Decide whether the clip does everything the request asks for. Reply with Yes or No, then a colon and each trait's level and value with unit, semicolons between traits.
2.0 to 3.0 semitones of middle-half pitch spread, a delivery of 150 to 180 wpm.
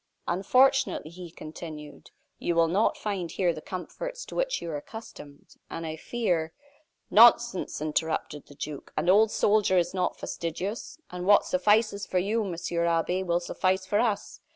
No: average, 4.2 semitones; average, 165 wpm